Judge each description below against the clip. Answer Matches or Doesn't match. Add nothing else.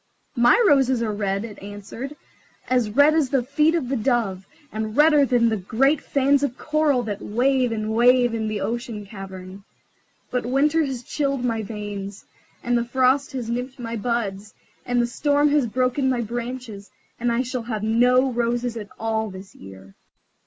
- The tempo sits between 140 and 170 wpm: Doesn't match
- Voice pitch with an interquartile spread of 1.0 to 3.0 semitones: Doesn't match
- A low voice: Doesn't match